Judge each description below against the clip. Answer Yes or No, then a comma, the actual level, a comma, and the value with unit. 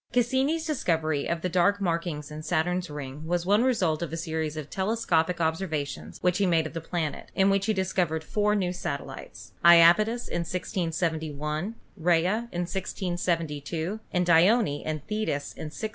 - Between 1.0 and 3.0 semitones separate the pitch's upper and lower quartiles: No, average, 3.6 semitones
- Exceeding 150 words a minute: Yes, average, 165 wpm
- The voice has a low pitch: No, medium, 175 Hz